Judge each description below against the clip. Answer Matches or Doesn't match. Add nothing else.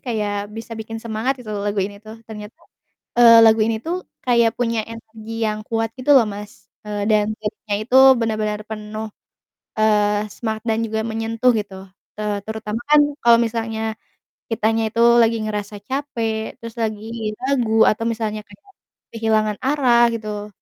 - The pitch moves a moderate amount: Doesn't match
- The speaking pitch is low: Doesn't match